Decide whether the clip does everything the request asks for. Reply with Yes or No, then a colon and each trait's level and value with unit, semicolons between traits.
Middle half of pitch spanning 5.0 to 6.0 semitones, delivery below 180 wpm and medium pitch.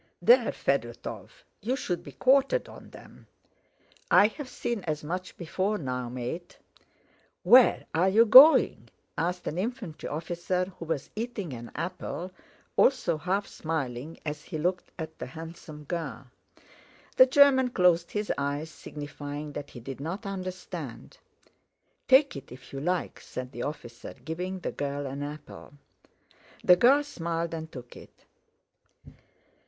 Yes: wide, 5.4 semitones; average, 140 wpm; medium, 170 Hz